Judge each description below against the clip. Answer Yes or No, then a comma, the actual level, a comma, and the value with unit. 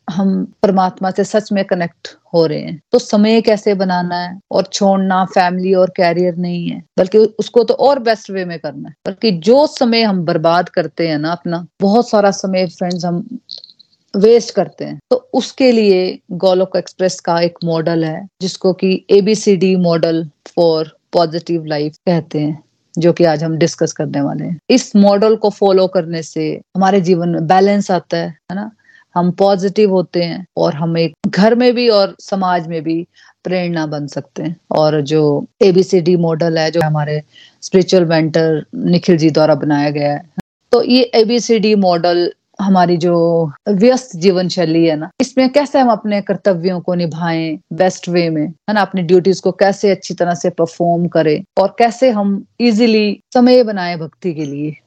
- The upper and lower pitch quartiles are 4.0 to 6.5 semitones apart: No, average, 3.4 semitones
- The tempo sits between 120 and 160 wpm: No, average, 175 wpm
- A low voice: No, medium, 185 Hz